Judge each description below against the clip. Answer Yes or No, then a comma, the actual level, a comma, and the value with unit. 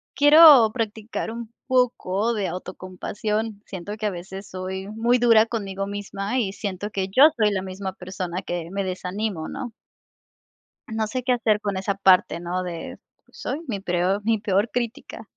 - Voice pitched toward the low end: No, high, 205 Hz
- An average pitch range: Yes, average, 3.1 semitones